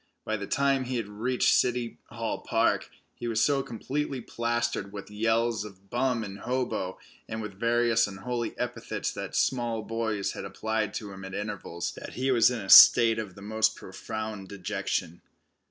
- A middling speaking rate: Yes, average, 170 wpm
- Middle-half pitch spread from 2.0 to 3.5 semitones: Yes, average, 2.8 semitones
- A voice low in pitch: Yes, low, 110 Hz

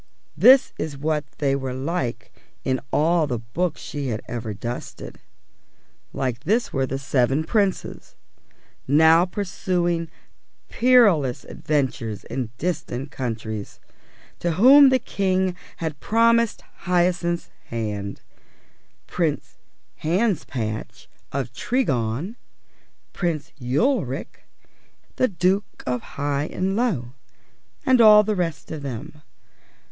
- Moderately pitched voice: Yes, medium, 155 Hz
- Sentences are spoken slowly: Yes, slow, 100 wpm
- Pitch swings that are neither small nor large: No, wide, 6.5 semitones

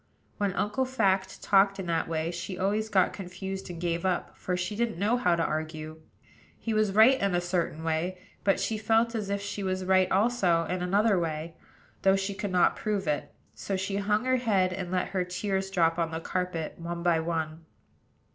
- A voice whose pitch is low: No, medium, 185 Hz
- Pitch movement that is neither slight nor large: Yes, average, 3.0 semitones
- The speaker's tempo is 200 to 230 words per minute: Yes, fast, 205 wpm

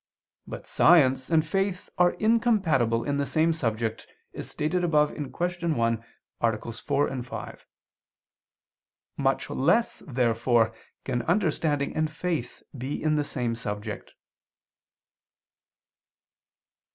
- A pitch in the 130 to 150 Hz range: Yes, medium, 140 Hz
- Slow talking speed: Yes, slow, 105 wpm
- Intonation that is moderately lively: No, wide, 5.7 semitones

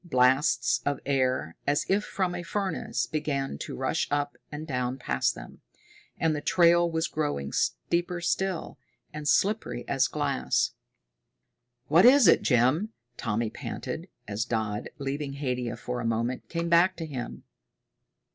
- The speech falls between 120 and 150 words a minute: Yes, average, 145 wpm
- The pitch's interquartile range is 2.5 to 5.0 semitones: No, wide, 5.4 semitones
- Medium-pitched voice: Yes, medium, 145 Hz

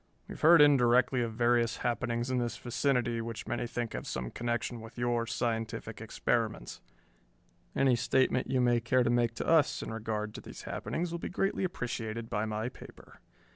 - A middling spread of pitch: No, narrow, 1.8 semitones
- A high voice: No, low, 120 Hz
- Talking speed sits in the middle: Yes, average, 180 wpm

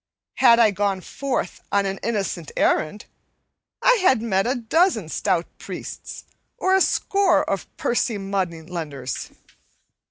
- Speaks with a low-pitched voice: No, high, 200 Hz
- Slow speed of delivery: Yes, slow, 130 wpm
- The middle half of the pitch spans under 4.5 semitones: No, average, 5.2 semitones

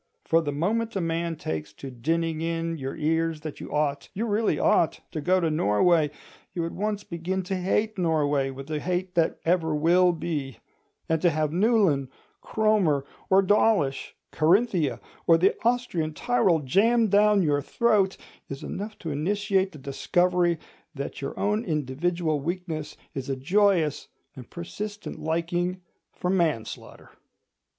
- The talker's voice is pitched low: No, medium, 170 Hz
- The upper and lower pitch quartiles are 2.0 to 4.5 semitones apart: Yes, average, 4.2 semitones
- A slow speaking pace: No, average, 150 wpm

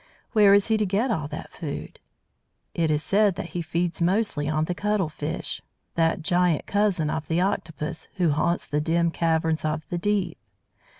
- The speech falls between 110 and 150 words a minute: No, average, 180 wpm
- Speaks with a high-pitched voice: No, medium, 170 Hz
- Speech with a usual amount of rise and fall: Yes, average, 3.8 semitones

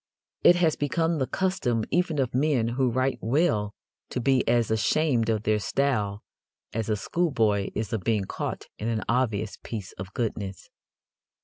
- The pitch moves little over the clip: No, average, 4.5 semitones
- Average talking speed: Yes, average, 165 wpm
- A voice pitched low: Yes, low, 115 Hz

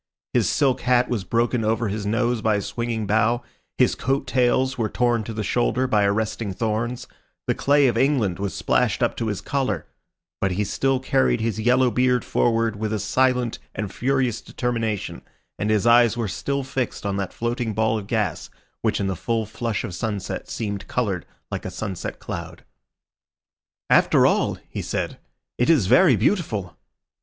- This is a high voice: No, low, 115 Hz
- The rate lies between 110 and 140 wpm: No, average, 175 wpm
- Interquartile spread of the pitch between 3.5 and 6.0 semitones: No, average, 3.0 semitones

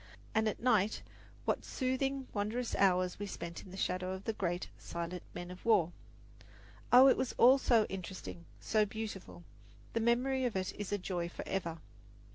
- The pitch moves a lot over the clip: No, average, 4.5 semitones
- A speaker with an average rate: Yes, average, 170 wpm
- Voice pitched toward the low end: No, high, 205 Hz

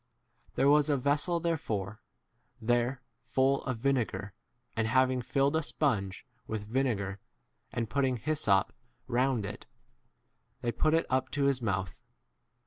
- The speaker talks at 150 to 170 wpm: No, slow, 135 wpm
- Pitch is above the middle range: No, low, 130 Hz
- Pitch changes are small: No, average, 4.0 semitones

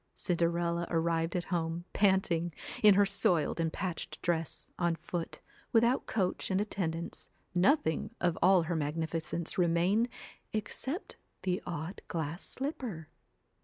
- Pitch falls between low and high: Yes, medium, 175 Hz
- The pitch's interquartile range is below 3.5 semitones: Yes, average, 2.8 semitones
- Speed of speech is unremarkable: No, slow, 125 wpm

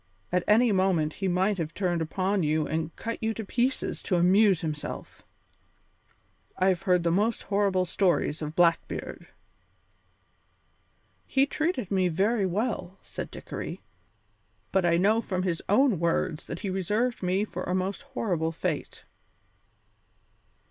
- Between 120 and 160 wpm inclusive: Yes, average, 140 wpm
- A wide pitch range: No, average, 3.6 semitones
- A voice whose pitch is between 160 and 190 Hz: Yes, medium, 185 Hz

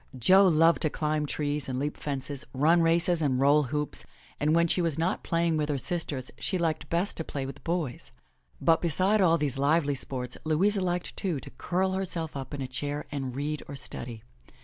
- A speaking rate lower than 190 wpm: No, average, 200 wpm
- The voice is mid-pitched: Yes, medium, 155 Hz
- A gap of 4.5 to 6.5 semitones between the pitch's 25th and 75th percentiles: No, average, 3.4 semitones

